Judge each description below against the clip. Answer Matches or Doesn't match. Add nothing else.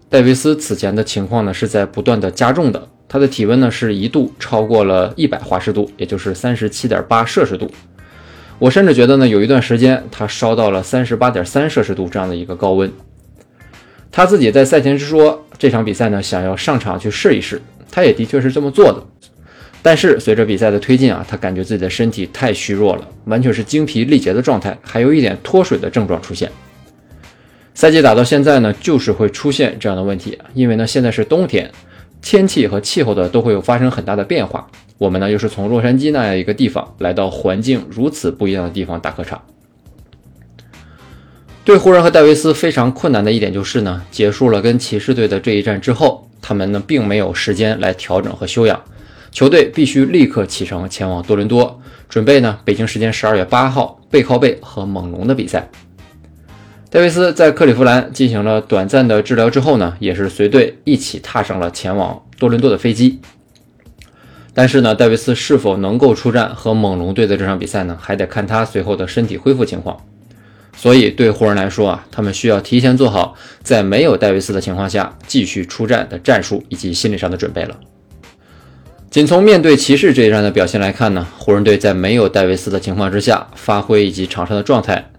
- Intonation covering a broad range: Doesn't match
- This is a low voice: Matches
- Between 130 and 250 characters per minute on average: Doesn't match